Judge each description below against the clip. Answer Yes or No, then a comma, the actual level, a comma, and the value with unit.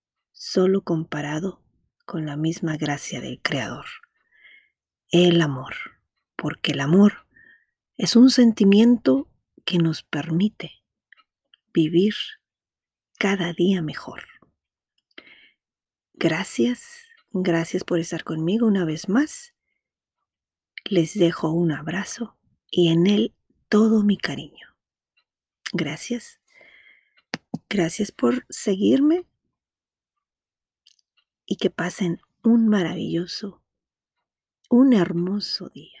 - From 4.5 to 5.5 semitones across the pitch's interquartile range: Yes, average, 5.0 semitones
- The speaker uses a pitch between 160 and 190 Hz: Yes, medium, 185 Hz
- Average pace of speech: No, slow, 90 wpm